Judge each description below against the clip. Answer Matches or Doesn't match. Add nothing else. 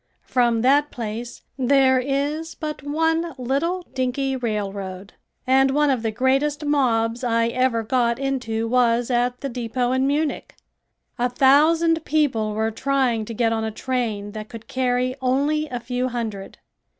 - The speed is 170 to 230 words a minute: Doesn't match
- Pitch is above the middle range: Matches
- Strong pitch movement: Doesn't match